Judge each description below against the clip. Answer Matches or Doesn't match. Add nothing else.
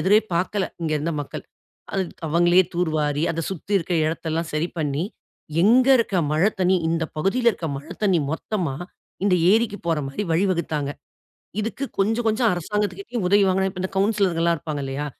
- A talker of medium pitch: Matches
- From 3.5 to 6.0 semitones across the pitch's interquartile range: Matches